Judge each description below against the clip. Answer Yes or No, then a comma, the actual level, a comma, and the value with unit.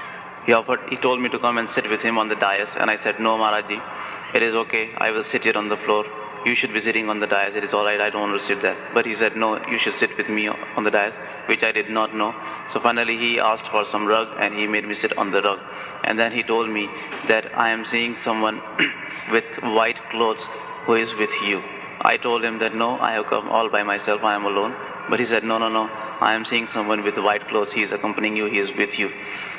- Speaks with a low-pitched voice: Yes, low, 110 Hz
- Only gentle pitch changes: Yes, narrow, 1.4 semitones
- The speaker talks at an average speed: No, fast, 265 wpm